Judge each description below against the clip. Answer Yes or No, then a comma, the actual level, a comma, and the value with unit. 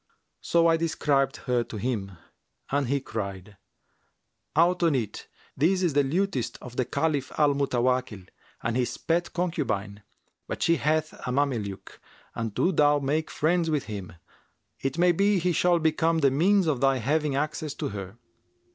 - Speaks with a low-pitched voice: No, medium, 145 Hz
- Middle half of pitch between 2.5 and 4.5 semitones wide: No, average, 5.0 semitones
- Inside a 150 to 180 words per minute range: Yes, average, 165 wpm